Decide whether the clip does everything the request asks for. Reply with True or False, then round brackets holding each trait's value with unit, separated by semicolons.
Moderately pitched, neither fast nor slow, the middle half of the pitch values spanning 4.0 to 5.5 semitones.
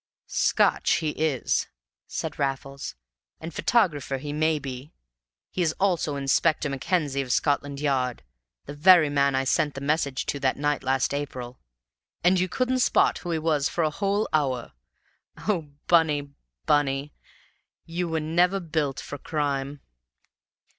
False (145 Hz; 145 wpm; 3.1 semitones)